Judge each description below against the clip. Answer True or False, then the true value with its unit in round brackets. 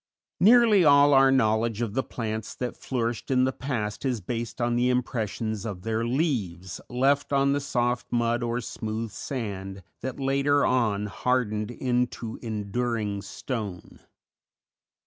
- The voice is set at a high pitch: False (120 Hz)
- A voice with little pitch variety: False (3.4 semitones)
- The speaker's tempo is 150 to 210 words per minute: False (140 wpm)